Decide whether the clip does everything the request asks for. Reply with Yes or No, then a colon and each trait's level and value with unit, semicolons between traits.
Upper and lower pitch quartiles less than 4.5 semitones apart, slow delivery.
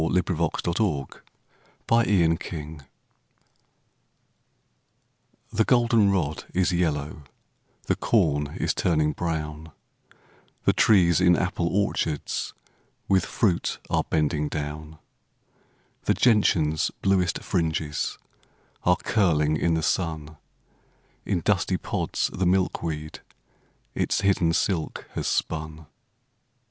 Yes: average, 3.4 semitones; slow, 95 wpm